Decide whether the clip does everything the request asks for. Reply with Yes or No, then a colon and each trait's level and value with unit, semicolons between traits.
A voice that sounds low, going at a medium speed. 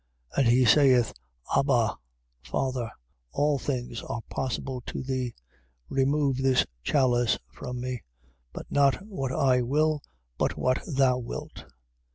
No: low, 130 Hz; slow, 130 wpm